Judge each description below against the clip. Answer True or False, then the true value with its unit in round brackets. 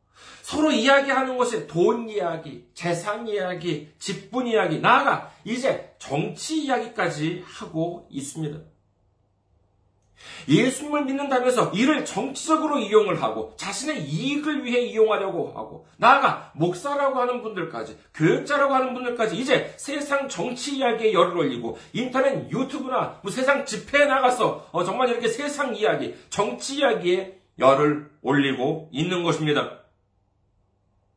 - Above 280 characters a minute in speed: True (310 characters per minute)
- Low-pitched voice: False (210 Hz)